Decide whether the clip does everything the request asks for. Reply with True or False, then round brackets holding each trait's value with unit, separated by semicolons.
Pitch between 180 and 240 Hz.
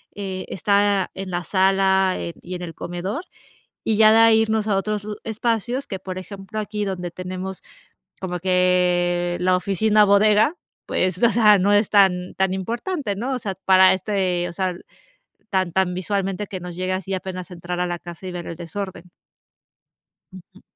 True (190 Hz)